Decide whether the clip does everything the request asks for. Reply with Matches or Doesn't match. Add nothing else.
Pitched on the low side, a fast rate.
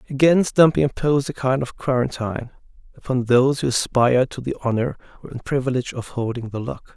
Doesn't match